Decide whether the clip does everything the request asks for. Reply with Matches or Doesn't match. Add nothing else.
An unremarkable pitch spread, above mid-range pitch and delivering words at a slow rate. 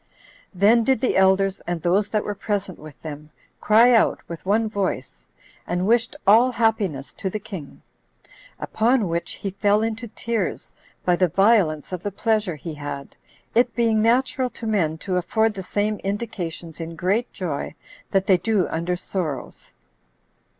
Doesn't match